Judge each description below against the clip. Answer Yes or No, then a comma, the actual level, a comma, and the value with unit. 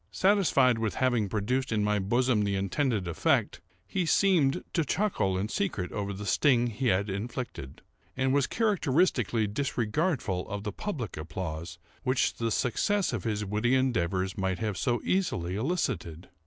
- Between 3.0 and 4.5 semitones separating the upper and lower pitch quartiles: No, wide, 5.6 semitones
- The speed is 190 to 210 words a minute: No, average, 155 wpm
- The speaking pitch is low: Yes, low, 115 Hz